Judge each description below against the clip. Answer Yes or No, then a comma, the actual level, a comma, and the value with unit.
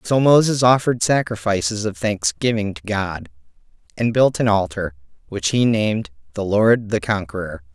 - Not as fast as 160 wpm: Yes, average, 145 wpm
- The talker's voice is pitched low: Yes, low, 105 Hz